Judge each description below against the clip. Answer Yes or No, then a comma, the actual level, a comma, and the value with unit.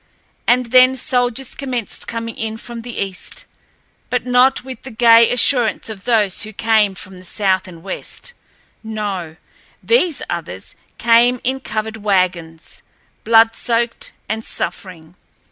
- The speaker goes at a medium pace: No, slow, 130 wpm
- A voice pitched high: Yes, high, 225 Hz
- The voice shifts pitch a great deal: No, average, 4.1 semitones